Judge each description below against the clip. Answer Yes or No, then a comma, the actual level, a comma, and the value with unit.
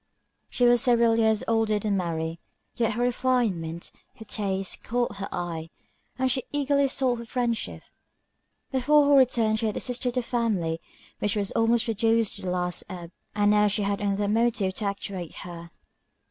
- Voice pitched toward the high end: Yes, high, 220 Hz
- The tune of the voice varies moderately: Yes, average, 3.8 semitones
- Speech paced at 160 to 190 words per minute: Yes, average, 170 wpm